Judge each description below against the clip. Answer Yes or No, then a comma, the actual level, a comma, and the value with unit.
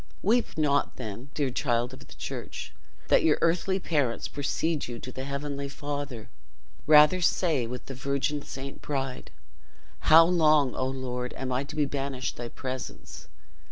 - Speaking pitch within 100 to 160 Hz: Yes, medium, 140 Hz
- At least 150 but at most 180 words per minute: Yes, average, 155 wpm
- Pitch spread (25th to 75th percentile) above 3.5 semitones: No, average, 2.8 semitones